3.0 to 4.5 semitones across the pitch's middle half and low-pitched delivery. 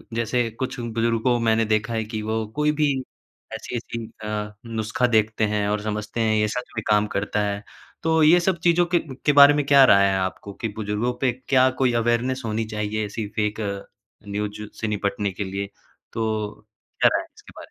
No: narrow, 2.6 semitones; low, 110 Hz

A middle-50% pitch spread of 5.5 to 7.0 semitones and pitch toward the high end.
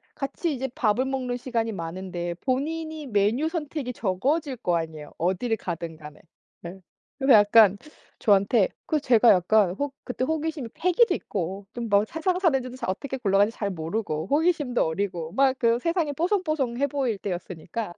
Yes: wide, 6.7 semitones; high, 235 Hz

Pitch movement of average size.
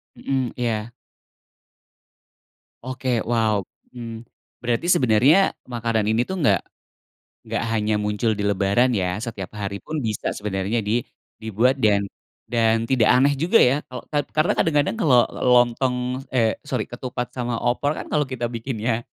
Yes: average, 3.0 semitones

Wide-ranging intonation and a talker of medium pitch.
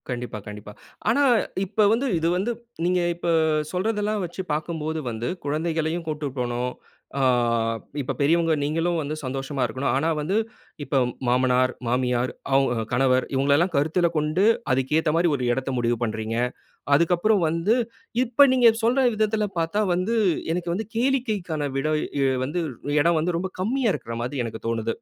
Yes: wide, 5.9 semitones; medium, 155 Hz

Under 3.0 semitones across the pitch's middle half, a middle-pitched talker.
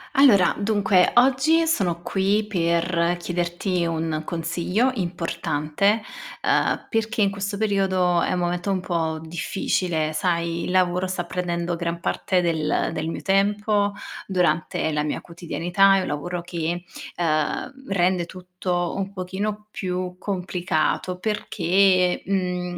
Yes: narrow, 2.5 semitones; medium, 180 Hz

